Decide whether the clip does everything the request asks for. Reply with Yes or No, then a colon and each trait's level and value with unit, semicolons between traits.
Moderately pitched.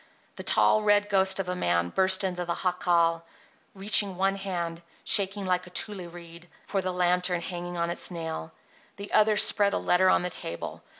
Yes: medium, 180 Hz